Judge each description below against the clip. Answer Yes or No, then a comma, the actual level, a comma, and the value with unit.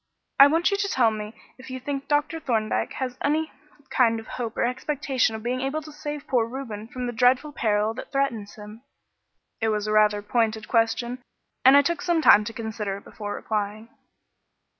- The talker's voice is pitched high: Yes, high, 240 Hz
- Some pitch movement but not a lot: Yes, average, 4.2 semitones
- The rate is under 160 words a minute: No, average, 195 wpm